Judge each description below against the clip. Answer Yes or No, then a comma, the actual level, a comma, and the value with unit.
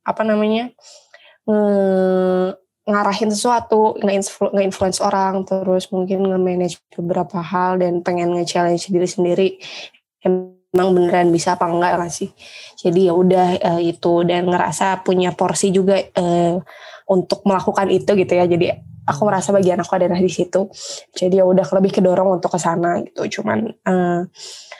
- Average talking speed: No, fast, 145 wpm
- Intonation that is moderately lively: No, narrow, 1.7 semitones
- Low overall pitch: No, medium, 185 Hz